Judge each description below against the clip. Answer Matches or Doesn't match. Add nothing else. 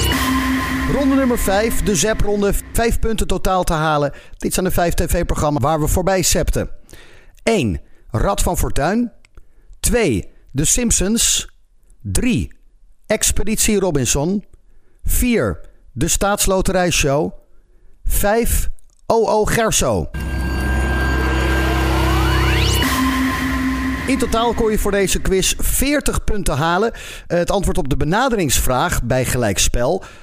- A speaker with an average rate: Doesn't match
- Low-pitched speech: Doesn't match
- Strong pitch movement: Matches